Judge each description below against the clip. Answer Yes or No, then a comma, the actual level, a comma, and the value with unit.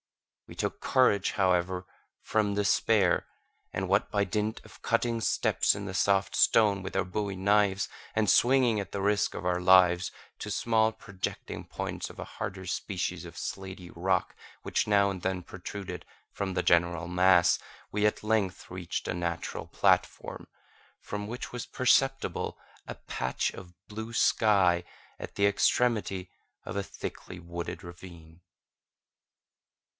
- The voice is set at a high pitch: No, very low, 95 Hz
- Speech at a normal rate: Yes, average, 145 wpm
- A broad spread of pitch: No, narrow, 2.6 semitones